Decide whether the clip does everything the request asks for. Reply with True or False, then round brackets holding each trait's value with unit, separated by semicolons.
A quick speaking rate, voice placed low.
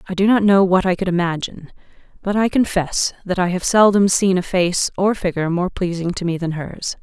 False (220 wpm; 185 Hz)